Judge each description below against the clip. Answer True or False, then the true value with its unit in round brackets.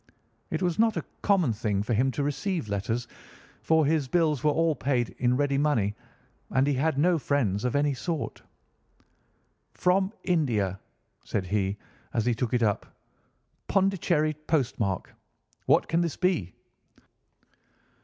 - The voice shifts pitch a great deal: True (6.1 semitones)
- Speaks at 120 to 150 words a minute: True (145 wpm)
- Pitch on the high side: False (140 Hz)